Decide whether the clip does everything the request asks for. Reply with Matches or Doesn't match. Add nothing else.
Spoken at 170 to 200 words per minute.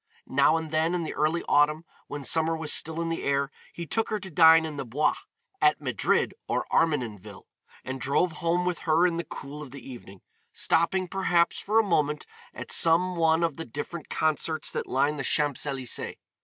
Matches